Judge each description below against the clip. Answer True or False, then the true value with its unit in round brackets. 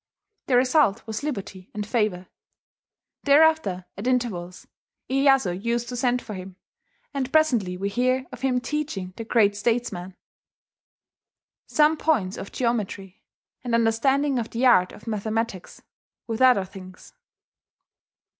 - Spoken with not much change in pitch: False (4.8 semitones)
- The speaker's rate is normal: False (125 wpm)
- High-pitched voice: True (230 Hz)